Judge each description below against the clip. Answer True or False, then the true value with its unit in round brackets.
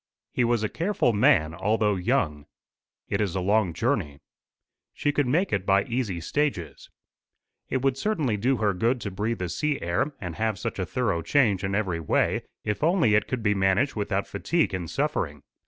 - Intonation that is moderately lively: False (5.8 semitones)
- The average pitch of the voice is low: True (105 Hz)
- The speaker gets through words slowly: False (190 wpm)